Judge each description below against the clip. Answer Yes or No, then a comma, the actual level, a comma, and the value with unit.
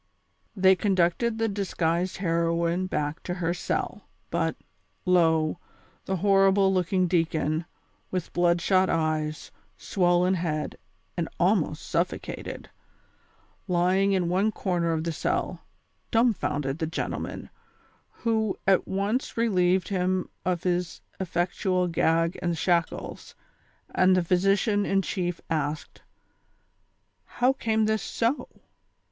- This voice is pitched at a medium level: Yes, medium, 180 Hz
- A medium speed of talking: No, slow, 115 wpm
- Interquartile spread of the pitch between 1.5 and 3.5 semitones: Yes, narrow, 2.6 semitones